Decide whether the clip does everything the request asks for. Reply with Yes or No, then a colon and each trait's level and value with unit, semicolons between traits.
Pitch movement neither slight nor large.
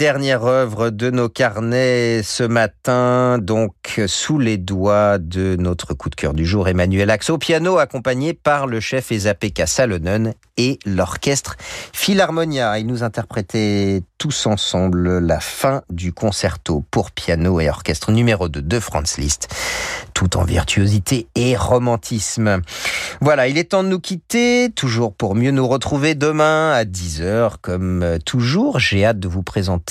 No: wide, 5.7 semitones